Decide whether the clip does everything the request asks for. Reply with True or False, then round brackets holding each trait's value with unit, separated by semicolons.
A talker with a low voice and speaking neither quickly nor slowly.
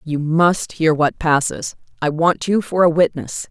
False (160 Hz; 190 wpm)